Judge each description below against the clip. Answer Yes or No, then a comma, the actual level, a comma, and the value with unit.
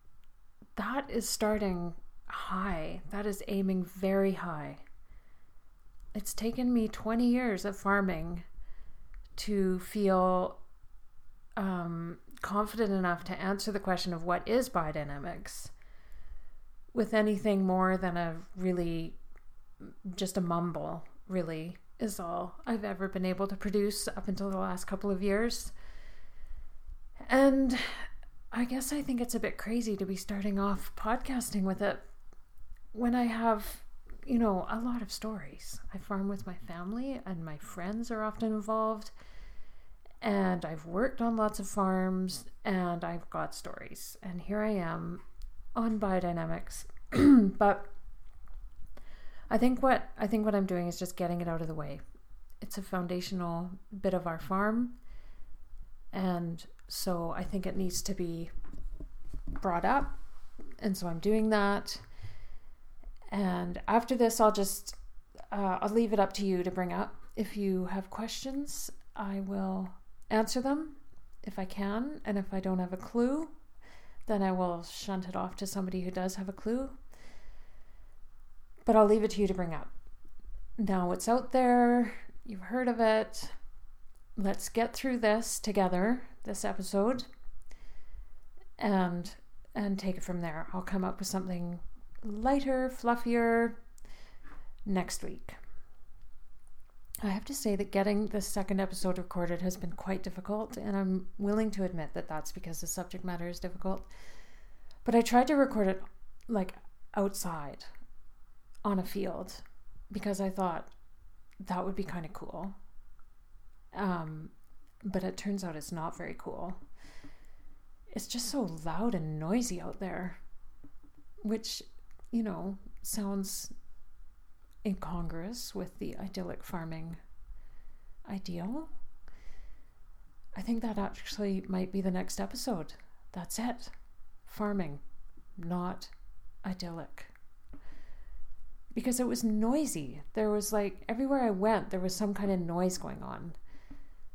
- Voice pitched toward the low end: No, high, 195 Hz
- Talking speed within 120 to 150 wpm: Yes, average, 140 wpm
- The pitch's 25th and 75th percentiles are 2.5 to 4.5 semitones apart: Yes, average, 3.4 semitones